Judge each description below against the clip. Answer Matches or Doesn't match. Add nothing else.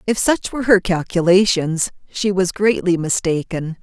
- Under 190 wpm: Matches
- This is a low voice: Doesn't match